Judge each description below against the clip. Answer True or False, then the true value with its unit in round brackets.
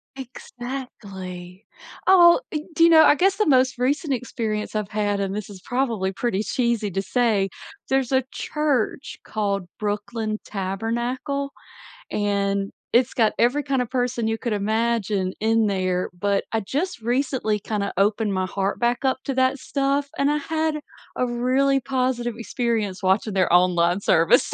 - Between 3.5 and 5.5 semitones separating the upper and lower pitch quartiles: True (4.7 semitones)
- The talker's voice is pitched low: False (230 Hz)